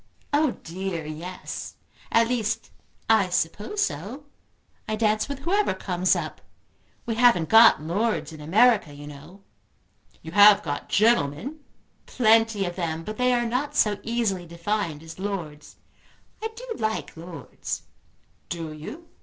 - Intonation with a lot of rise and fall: Yes, wide, 5.9 semitones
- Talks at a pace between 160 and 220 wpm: No, slow, 135 wpm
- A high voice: Yes, high, 205 Hz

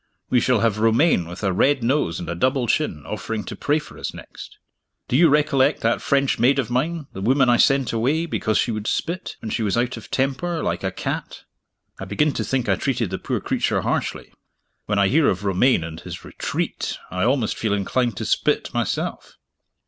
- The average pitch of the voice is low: Yes, low, 120 Hz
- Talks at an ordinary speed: No, fast, 210 wpm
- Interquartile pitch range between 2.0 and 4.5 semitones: No, average, 5.2 semitones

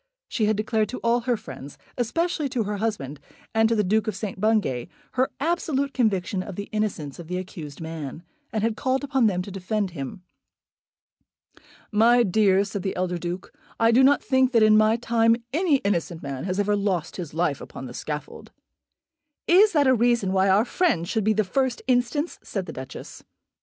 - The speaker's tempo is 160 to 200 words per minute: Yes, average, 195 wpm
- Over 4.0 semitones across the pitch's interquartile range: Yes, average, 4.9 semitones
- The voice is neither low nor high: No, high, 215 Hz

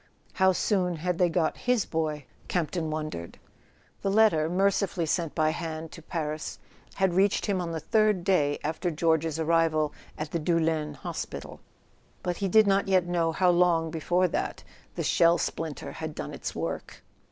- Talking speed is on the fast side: No, average, 170 wpm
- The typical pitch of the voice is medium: Yes, medium, 170 Hz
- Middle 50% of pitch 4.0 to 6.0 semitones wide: No, average, 2.7 semitones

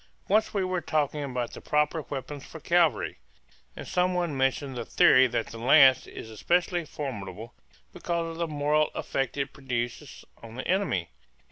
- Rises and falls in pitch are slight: No, average, 5.0 semitones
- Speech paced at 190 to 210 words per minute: No, average, 165 wpm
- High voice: No, medium, 145 Hz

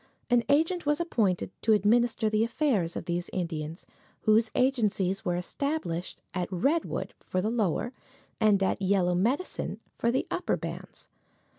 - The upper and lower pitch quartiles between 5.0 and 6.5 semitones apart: Yes, average, 5.3 semitones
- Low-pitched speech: No, high, 215 Hz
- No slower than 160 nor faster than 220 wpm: No, average, 145 wpm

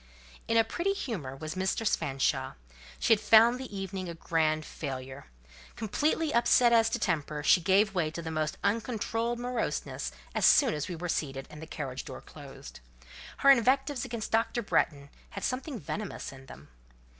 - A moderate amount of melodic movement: No, wide, 7.3 semitones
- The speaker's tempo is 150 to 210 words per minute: Yes, average, 170 wpm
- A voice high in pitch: Yes, high, 195 Hz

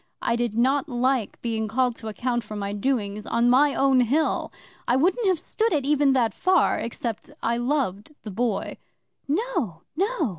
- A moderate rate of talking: Yes, average, 175 wpm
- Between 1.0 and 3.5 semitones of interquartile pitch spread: No, average, 4.6 semitones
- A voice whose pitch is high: Yes, very high, 250 Hz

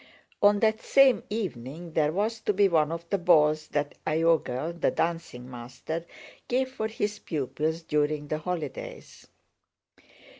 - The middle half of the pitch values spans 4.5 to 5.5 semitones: Yes, average, 5.2 semitones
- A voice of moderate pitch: Yes, medium, 165 Hz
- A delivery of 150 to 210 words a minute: No, average, 140 wpm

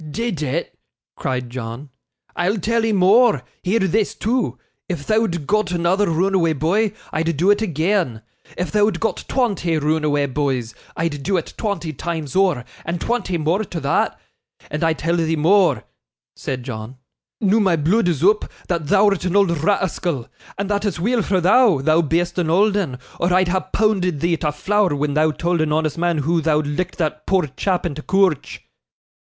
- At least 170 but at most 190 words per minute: Yes, average, 180 wpm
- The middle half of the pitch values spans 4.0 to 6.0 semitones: Yes, average, 4.5 semitones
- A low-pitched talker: No, medium, 175 Hz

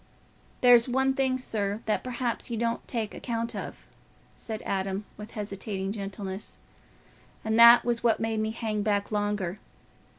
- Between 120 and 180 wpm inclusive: Yes, average, 145 wpm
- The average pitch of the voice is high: Yes, high, 220 Hz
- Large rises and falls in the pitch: No, narrow, 2.4 semitones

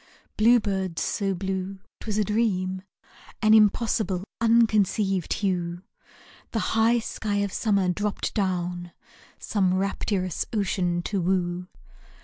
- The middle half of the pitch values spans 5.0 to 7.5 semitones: No, average, 2.7 semitones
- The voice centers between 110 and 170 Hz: No, high, 195 Hz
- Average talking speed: No, slow, 120 wpm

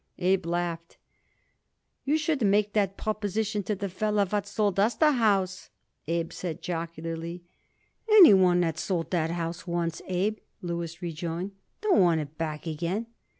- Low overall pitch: No, medium, 180 Hz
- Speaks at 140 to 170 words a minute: Yes, average, 150 wpm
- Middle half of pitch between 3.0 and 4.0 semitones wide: Yes, average, 3.7 semitones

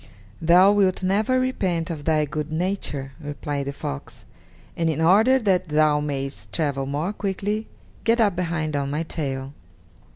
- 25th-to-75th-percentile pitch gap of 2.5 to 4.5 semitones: No, average, 4.9 semitones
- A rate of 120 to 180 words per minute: Yes, average, 155 wpm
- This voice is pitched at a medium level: Yes, medium, 160 Hz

